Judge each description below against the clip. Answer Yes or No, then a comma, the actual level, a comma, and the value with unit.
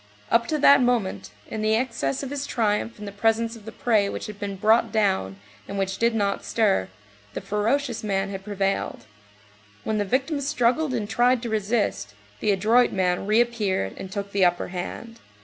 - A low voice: No, high, 215 Hz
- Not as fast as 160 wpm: No, average, 185 wpm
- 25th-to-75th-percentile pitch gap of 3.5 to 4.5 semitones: No, average, 3.1 semitones